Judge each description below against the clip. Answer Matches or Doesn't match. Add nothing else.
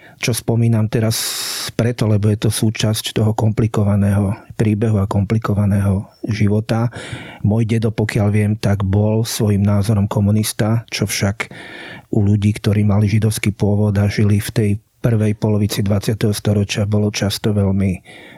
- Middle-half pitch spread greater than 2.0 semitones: Doesn't match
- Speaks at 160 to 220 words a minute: Doesn't match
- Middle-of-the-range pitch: Doesn't match